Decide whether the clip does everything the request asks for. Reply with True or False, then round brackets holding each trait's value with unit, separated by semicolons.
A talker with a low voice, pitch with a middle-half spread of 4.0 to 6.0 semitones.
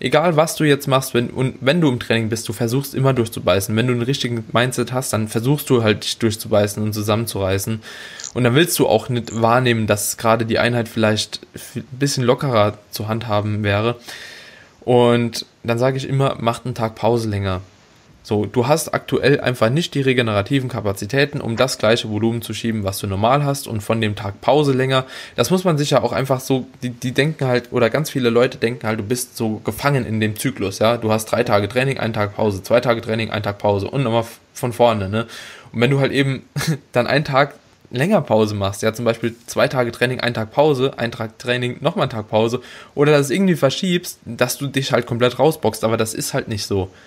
False (120 Hz; 3.3 semitones)